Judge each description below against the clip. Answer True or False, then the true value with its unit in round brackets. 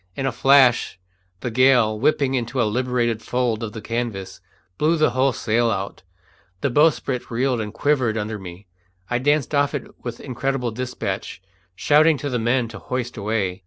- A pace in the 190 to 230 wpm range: False (170 wpm)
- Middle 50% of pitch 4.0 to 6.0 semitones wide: False (3.3 semitones)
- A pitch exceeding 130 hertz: False (120 Hz)